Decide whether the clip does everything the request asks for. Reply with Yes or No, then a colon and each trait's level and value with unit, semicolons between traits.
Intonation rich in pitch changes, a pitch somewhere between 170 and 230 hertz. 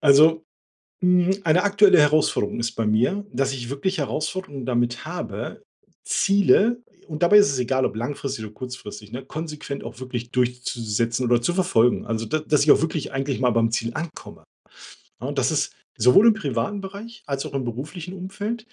No: wide, 6.7 semitones; medium, 140 Hz